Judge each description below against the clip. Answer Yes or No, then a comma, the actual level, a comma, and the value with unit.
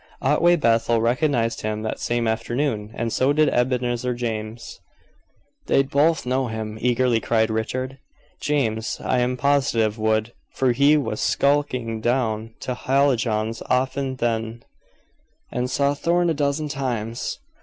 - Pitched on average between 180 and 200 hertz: No, low, 125 Hz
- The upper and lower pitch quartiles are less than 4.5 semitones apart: Yes, average, 3.5 semitones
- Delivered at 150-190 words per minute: No, slow, 135 wpm